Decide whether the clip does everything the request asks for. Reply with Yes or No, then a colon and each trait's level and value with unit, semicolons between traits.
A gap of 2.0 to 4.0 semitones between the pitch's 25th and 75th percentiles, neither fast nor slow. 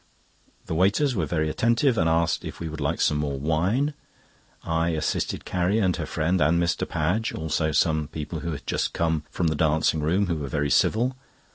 Yes: average, 3.0 semitones; average, 195 wpm